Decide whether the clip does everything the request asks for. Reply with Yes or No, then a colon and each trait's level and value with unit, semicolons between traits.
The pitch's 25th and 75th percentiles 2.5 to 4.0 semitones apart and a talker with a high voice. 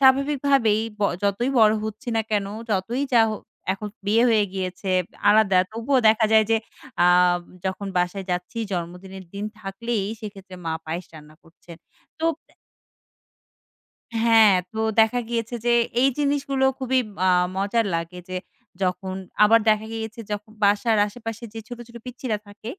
Yes: average, 3.5 semitones; high, 215 Hz